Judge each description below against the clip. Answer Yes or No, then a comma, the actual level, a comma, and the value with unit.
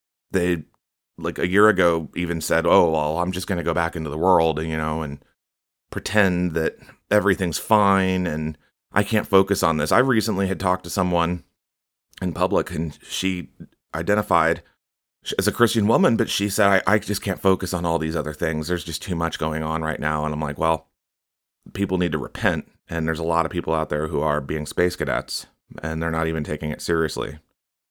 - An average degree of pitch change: Yes, average, 3.3 semitones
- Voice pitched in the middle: No, very low, 85 Hz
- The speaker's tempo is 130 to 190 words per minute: No, fast, 205 wpm